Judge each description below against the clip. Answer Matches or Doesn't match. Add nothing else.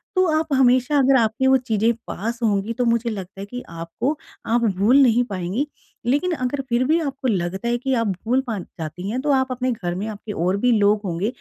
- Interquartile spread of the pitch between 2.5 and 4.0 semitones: Doesn't match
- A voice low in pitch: Doesn't match